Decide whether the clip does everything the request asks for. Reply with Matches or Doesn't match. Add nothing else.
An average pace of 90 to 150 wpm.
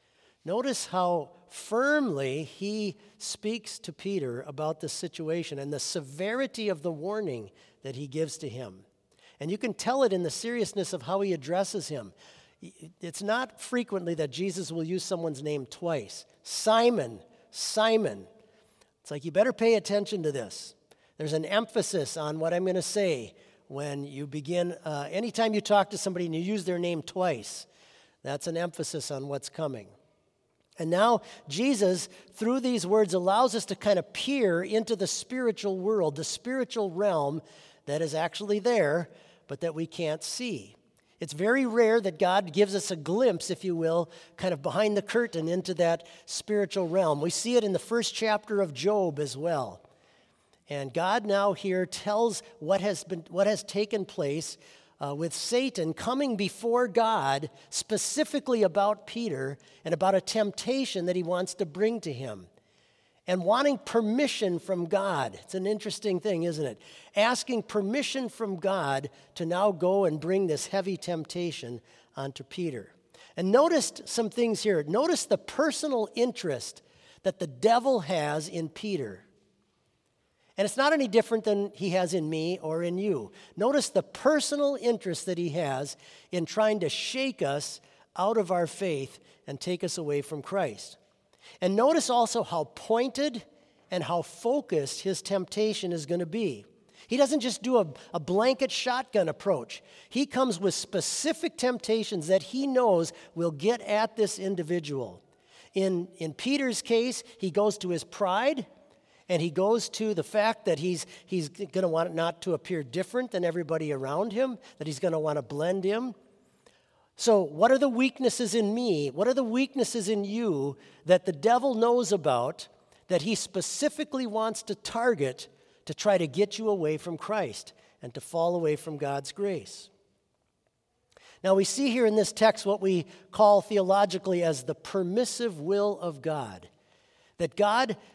Doesn't match